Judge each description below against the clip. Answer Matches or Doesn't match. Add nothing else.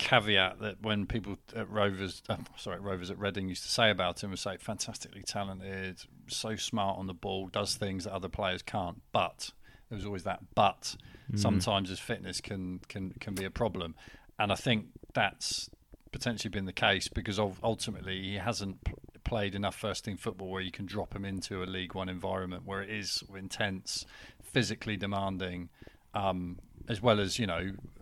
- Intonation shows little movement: Matches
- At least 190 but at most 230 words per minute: Doesn't match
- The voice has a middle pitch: Doesn't match